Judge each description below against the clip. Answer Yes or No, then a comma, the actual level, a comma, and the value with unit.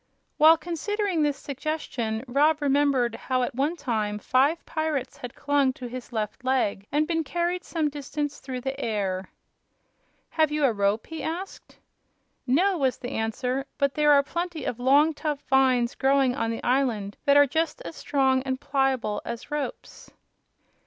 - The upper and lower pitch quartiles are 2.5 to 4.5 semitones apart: Yes, average, 3.6 semitones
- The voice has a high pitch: Yes, very high, 275 Hz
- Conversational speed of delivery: Yes, average, 165 wpm